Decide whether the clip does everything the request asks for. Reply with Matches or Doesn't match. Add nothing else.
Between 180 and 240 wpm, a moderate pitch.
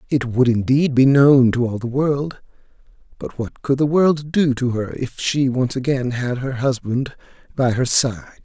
Doesn't match